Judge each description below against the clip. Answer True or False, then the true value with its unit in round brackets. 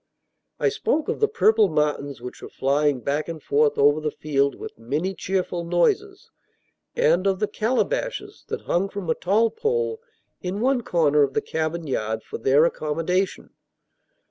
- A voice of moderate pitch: True (170 Hz)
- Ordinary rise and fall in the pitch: False (6.6 semitones)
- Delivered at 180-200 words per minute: False (165 wpm)